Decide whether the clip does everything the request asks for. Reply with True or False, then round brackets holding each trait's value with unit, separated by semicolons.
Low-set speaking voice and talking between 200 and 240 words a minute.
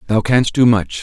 True (110 Hz; 235 wpm)